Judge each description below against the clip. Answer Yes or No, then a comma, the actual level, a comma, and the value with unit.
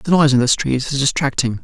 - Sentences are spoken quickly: Yes, fast, 260 wpm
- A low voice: Yes, low, 130 Hz